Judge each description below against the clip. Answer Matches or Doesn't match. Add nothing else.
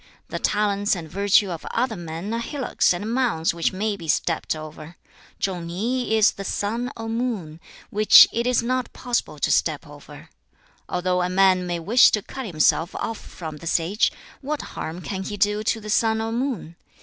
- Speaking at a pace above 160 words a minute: Matches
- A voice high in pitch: Matches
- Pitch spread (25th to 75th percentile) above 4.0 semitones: Matches